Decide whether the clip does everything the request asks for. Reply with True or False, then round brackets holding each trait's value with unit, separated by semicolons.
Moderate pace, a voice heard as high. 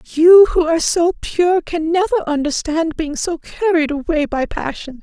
True (165 wpm; 330 Hz)